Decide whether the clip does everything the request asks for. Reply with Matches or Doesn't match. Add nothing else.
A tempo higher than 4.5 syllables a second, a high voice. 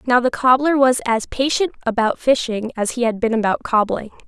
Matches